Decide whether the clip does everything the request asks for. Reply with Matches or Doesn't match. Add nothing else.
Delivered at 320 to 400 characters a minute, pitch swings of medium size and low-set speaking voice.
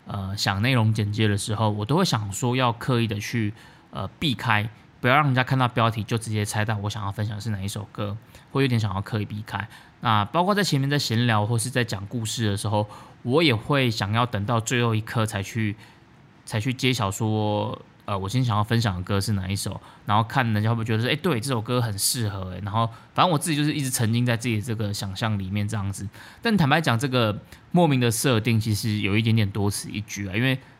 Matches